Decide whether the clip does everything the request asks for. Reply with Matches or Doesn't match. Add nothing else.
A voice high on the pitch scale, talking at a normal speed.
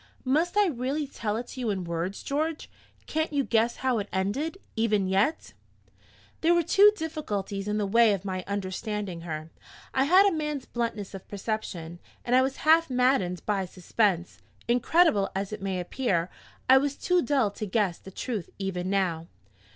Matches